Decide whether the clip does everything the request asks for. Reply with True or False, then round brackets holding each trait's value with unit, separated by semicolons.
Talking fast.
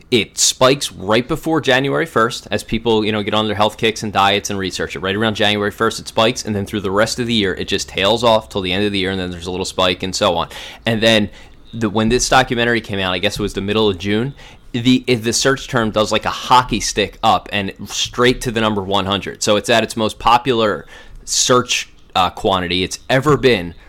True (245 wpm)